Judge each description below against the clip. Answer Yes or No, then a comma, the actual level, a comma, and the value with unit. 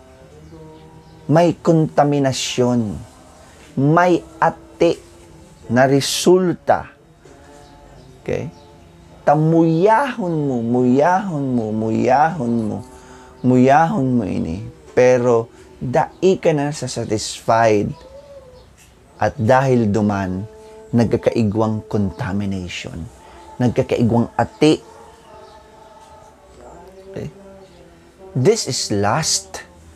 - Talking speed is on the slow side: Yes, slow, 65 wpm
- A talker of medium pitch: No, low, 125 Hz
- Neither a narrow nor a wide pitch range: No, wide, 7.4 semitones